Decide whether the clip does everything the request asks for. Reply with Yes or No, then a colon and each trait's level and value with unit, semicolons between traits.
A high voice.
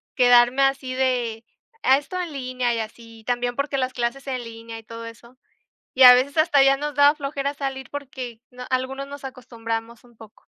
Yes: very high, 255 Hz